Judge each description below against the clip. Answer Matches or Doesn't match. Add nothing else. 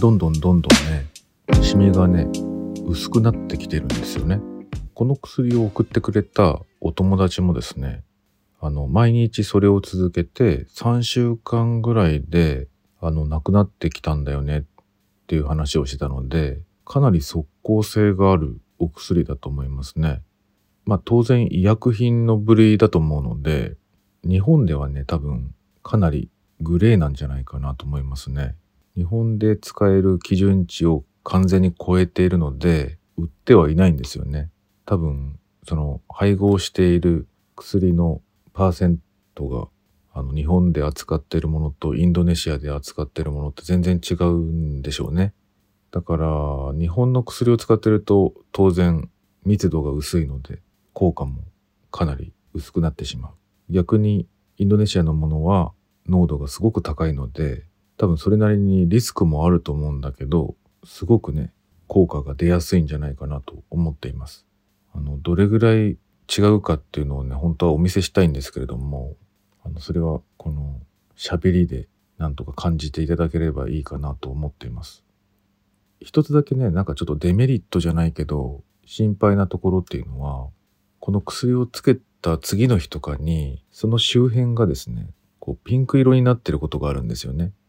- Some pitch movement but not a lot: Matches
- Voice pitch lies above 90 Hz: Doesn't match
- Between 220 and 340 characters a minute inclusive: Matches